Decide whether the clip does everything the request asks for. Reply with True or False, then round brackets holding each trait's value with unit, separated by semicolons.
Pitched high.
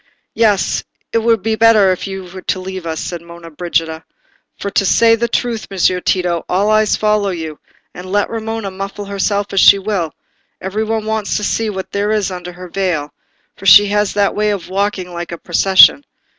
True (195 Hz)